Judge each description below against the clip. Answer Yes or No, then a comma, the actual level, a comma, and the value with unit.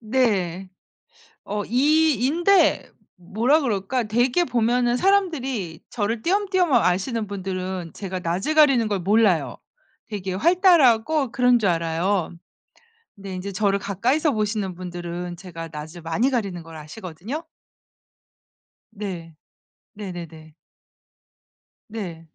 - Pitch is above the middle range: Yes, high, 205 Hz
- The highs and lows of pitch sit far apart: Yes, wide, 5.8 semitones